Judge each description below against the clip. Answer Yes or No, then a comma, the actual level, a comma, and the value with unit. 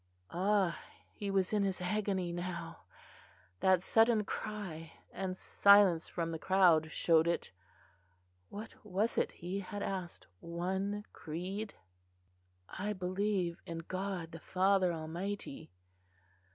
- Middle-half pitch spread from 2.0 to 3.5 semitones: Yes, average, 2.8 semitones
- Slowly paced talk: Yes, slow, 115 wpm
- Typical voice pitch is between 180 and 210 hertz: Yes, medium, 185 Hz